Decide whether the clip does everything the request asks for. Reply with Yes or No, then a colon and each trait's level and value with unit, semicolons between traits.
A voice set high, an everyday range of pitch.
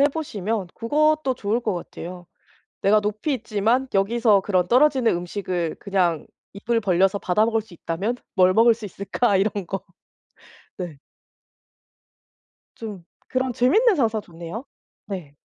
Yes: high, 210 Hz; average, 4.3 semitones